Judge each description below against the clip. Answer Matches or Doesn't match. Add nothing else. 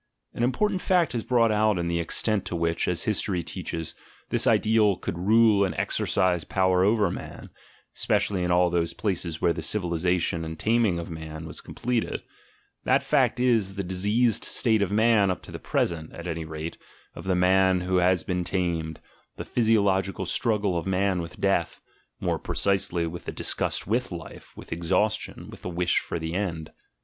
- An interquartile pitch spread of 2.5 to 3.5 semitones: Doesn't match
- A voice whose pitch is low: Matches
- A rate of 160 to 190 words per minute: Matches